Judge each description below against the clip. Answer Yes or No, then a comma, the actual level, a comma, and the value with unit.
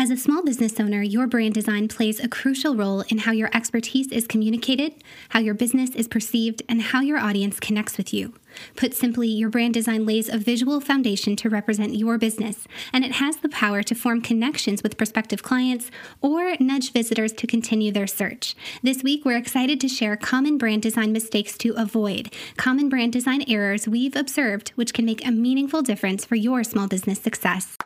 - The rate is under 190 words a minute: No, average, 195 wpm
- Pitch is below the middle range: No, high, 230 Hz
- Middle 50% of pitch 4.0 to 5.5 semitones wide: No, average, 2.8 semitones